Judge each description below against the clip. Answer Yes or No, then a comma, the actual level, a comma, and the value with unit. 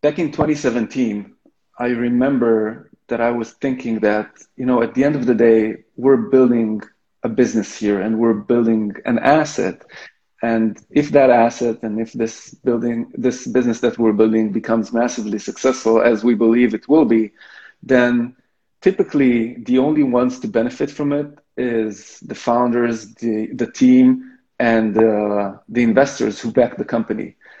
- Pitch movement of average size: No, narrow, 2.3 semitones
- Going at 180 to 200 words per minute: No, average, 160 wpm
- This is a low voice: Yes, low, 120 Hz